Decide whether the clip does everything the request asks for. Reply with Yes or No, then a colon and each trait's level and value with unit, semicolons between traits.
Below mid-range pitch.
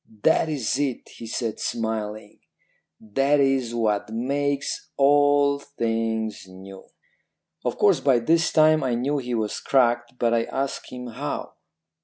Yes: low, 120 Hz